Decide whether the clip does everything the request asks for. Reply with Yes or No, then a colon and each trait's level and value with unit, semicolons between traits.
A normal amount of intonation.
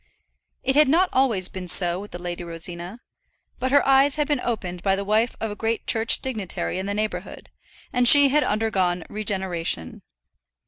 No: wide, 6.2 semitones